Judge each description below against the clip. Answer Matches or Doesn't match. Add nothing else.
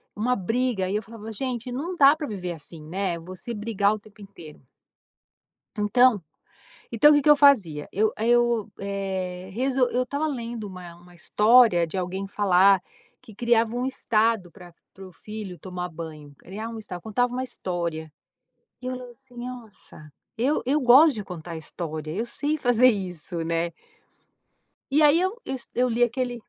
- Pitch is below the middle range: Doesn't match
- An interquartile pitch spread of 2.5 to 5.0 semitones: Doesn't match